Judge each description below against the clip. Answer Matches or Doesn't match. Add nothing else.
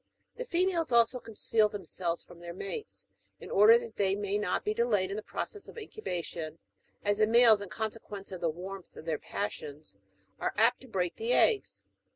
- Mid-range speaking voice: Doesn't match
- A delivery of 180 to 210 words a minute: Matches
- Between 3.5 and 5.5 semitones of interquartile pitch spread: Matches